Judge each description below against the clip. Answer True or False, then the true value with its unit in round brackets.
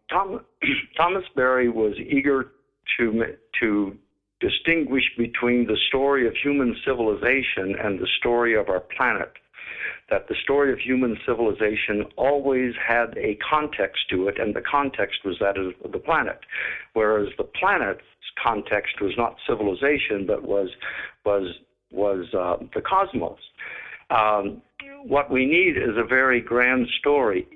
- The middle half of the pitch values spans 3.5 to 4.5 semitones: False (4.9 semitones)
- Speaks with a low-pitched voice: True (120 Hz)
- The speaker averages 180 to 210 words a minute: False (135 wpm)